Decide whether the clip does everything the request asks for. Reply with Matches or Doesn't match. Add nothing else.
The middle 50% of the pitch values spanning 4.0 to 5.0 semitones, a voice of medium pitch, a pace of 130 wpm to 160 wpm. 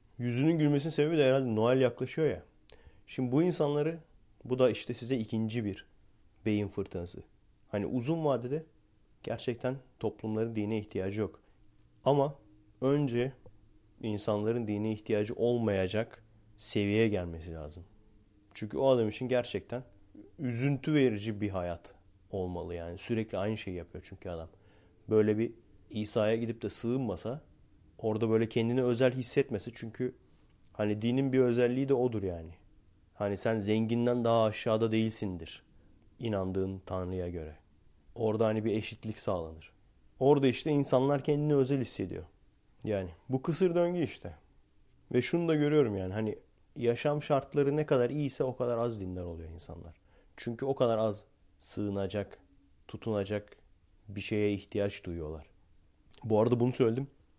Doesn't match